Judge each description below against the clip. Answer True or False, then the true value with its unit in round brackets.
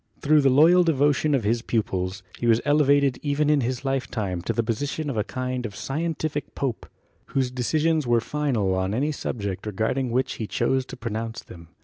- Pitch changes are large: False (4.4 semitones)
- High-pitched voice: False (130 Hz)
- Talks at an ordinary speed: False (210 wpm)